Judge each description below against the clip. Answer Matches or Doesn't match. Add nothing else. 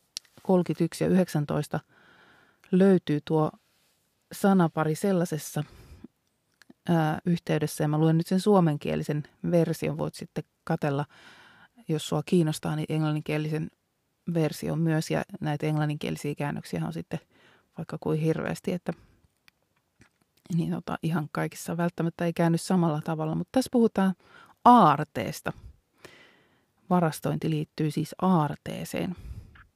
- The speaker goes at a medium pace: Matches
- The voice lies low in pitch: Doesn't match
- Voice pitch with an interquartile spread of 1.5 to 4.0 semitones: Matches